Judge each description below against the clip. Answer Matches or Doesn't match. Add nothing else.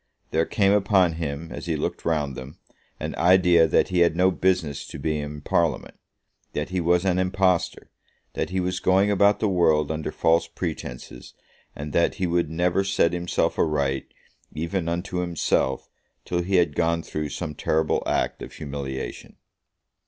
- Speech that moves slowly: Doesn't match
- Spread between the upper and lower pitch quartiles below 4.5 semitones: Matches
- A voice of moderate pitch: Doesn't match